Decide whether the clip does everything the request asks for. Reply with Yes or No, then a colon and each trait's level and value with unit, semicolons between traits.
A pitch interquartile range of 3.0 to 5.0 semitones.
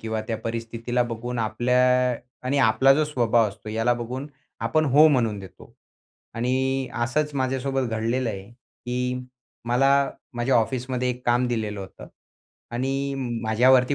No: narrow, 2.6 semitones